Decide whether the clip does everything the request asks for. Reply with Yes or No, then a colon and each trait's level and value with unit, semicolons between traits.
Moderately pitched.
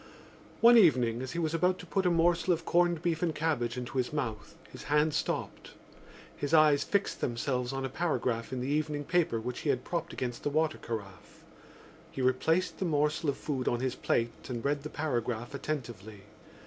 Yes: medium, 145 Hz